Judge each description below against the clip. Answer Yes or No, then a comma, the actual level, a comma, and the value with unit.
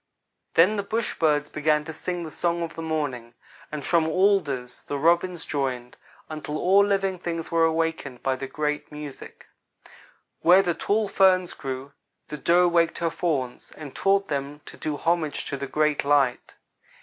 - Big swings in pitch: No, average, 3.4 semitones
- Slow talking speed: No, average, 170 wpm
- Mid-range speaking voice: Yes, medium, 160 Hz